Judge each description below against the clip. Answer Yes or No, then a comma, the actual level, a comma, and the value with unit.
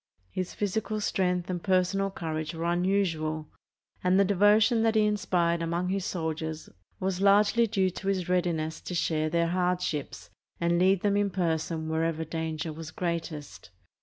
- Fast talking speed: No, average, 160 wpm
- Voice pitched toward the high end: No, medium, 180 Hz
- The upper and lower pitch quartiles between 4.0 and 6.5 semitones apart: No, average, 3.3 semitones